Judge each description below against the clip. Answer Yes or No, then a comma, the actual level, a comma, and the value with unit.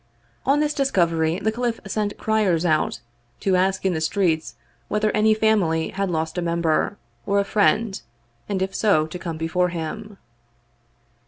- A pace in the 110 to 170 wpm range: Yes, average, 160 wpm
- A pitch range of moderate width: Yes, average, 4.4 semitones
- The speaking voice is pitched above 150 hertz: Yes, high, 190 Hz